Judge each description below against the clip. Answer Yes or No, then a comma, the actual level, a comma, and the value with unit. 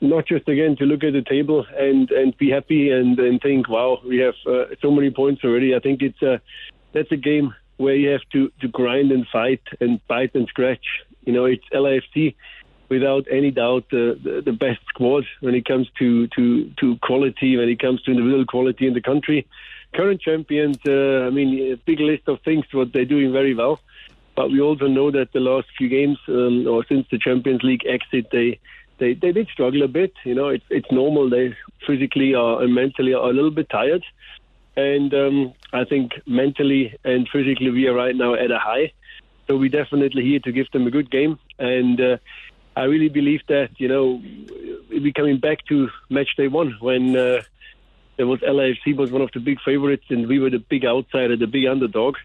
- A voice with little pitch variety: Yes, narrow, 2.1 semitones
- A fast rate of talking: Yes, fast, 210 wpm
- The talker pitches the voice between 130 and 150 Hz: Yes, low, 135 Hz